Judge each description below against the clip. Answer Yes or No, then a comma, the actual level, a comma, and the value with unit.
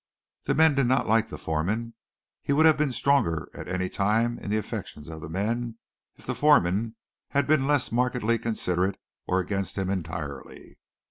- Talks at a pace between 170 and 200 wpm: Yes, average, 180 wpm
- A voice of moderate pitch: No, low, 110 Hz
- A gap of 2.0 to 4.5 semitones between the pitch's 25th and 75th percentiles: No, wide, 5.4 semitones